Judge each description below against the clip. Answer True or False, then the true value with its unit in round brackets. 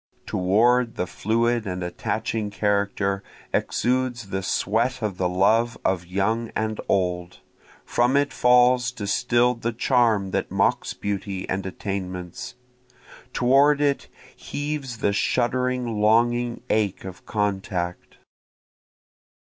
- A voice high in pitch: False (110 Hz)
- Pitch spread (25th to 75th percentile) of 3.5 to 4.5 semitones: True (4.0 semitones)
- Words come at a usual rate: False (110 wpm)